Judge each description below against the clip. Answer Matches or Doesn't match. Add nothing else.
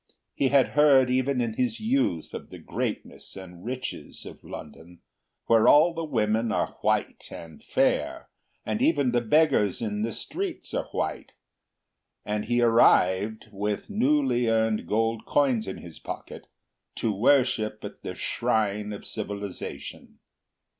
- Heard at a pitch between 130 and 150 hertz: Doesn't match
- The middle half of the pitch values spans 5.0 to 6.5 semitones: Doesn't match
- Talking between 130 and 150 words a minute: Matches